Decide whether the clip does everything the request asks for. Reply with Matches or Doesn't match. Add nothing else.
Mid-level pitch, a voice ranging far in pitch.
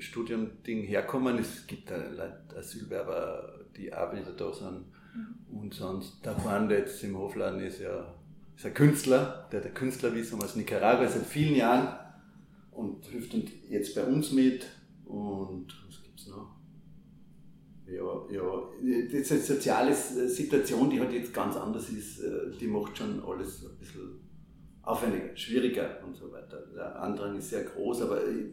Doesn't match